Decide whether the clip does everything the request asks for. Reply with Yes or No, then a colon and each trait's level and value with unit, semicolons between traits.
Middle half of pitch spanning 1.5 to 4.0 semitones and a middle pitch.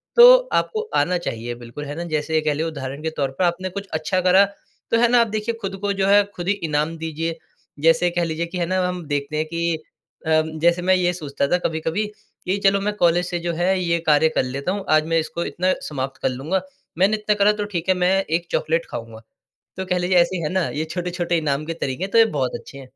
Yes: average, 3.4 semitones; medium, 170 Hz